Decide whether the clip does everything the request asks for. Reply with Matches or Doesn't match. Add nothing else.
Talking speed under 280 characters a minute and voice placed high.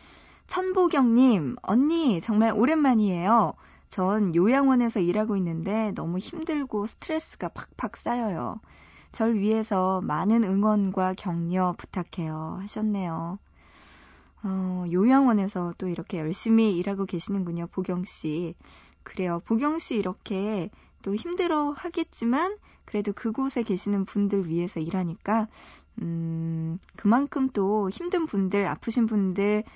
Matches